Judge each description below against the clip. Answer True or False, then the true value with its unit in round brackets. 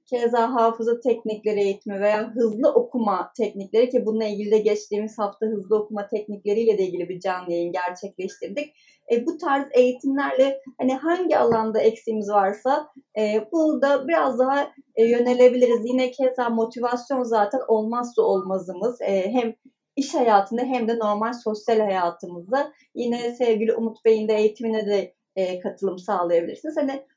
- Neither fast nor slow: False (145 wpm)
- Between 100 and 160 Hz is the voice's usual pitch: False (225 Hz)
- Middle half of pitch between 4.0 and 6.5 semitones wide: False (3.5 semitones)